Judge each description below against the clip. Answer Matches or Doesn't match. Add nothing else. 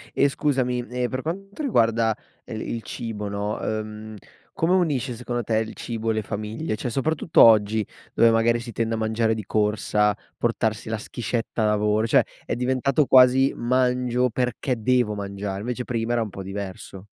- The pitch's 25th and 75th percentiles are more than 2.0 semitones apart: Matches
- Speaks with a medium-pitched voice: Doesn't match